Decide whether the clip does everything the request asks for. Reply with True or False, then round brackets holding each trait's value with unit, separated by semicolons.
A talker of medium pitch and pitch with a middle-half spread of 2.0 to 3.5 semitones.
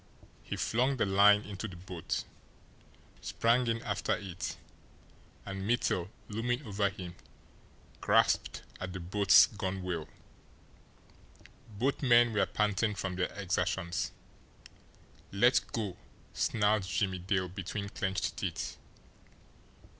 False (100 Hz; 3.0 semitones)